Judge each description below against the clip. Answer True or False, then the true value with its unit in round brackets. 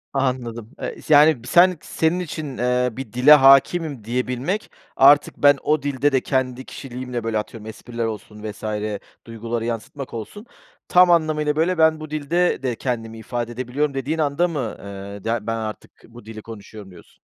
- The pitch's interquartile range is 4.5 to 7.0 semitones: True (4.8 semitones)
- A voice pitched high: False (130 Hz)